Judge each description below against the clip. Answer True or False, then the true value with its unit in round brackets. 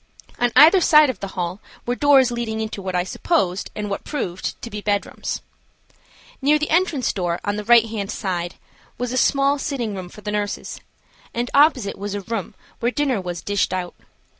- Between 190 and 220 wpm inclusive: True (195 wpm)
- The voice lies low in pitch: False (220 Hz)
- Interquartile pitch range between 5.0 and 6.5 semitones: True (5.4 semitones)